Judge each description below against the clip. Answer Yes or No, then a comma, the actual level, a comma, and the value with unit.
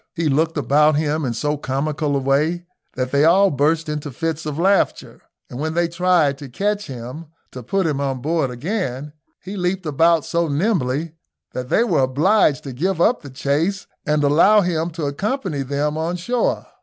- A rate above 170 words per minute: Yes, average, 185 wpm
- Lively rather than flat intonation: No, average, 3.8 semitones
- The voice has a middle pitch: Yes, medium, 155 Hz